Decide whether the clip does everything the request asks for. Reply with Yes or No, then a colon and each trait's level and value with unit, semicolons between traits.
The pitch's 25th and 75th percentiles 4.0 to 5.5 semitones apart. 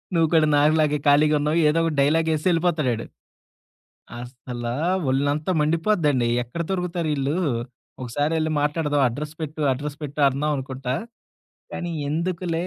No: average, 2.8 semitones